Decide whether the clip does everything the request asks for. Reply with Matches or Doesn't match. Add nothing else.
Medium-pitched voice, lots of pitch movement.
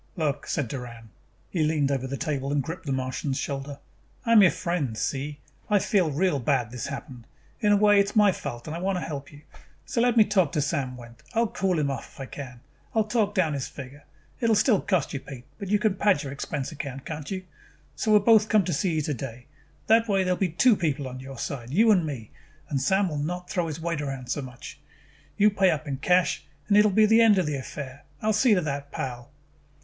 Matches